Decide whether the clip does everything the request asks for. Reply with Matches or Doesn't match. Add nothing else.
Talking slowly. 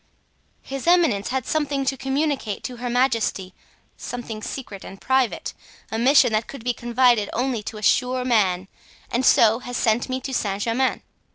Doesn't match